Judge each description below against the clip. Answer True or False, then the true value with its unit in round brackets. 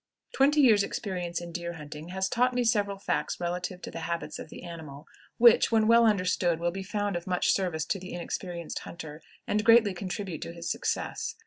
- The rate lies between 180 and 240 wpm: True (200 wpm)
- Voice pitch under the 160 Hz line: False (185 Hz)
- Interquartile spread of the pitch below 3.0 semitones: False (3.7 semitones)